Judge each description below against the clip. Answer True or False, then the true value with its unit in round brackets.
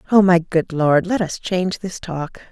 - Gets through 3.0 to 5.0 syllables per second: True (4.6 syllables/s)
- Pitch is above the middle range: False (175 Hz)